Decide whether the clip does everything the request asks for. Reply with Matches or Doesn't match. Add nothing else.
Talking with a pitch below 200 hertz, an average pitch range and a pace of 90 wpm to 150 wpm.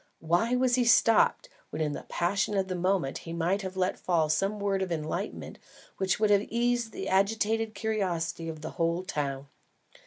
Doesn't match